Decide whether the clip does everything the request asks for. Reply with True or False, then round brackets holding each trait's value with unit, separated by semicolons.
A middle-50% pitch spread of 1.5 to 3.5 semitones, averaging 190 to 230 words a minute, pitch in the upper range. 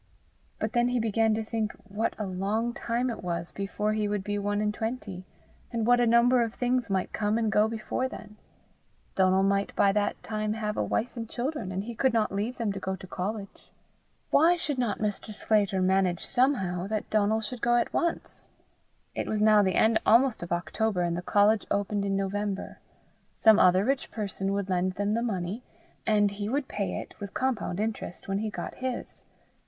True (2.8 semitones; 200 wpm; 210 Hz)